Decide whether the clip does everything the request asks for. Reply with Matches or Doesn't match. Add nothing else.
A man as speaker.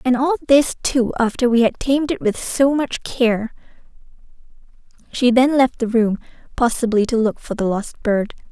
Doesn't match